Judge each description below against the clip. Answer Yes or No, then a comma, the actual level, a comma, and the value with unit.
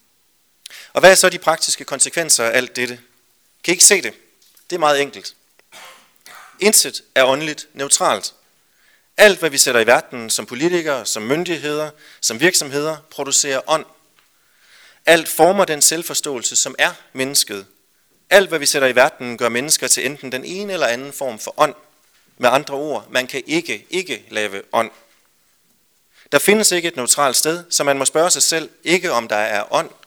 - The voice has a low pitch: No, medium, 150 Hz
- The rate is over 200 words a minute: No, average, 175 wpm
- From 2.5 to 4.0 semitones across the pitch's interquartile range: No, average, 4.4 semitones